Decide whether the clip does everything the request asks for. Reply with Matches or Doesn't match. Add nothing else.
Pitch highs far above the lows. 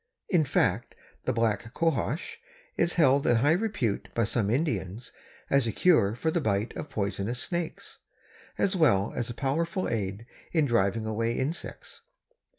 Matches